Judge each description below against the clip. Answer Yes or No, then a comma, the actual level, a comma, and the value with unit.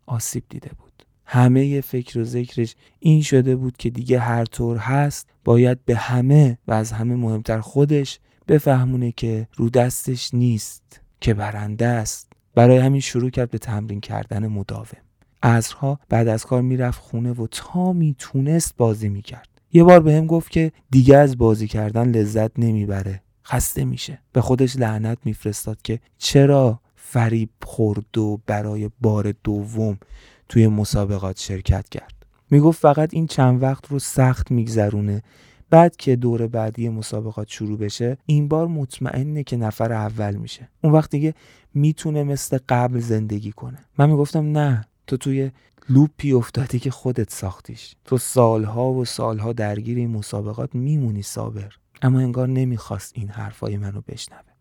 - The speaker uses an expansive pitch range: No, average, 3.5 semitones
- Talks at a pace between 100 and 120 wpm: No, average, 150 wpm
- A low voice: Yes, low, 120 Hz